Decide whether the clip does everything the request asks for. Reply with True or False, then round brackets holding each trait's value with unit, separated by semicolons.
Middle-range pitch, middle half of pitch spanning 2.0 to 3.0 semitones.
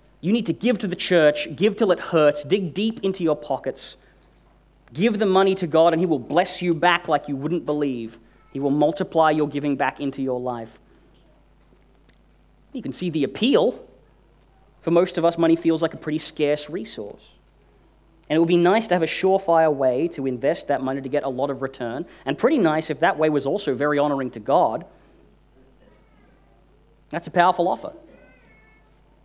False (155 Hz; 3.7 semitones)